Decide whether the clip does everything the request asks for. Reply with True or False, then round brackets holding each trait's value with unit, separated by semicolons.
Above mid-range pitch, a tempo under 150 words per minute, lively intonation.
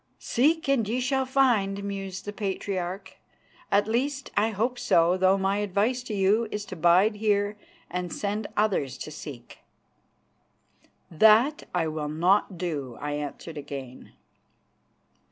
False (200 Hz; 135 wpm; 4.2 semitones)